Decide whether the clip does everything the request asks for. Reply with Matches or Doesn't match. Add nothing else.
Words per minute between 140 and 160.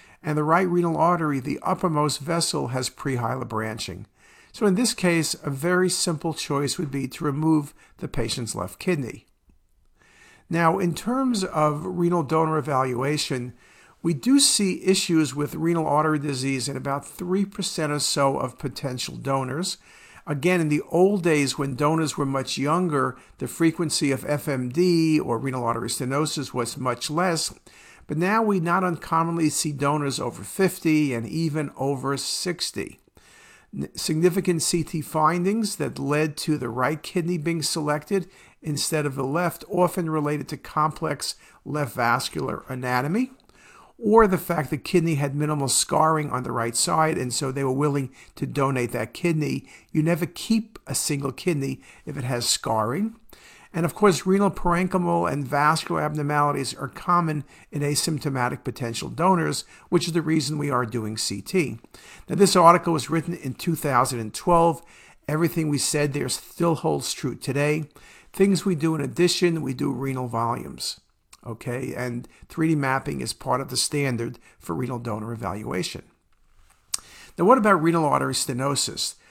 Matches